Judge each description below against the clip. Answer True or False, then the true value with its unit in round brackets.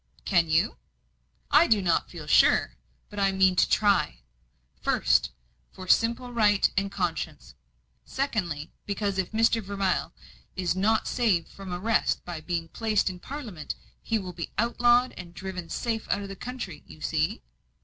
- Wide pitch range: False (4.0 semitones)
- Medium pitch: False (195 Hz)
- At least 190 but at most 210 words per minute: False (155 wpm)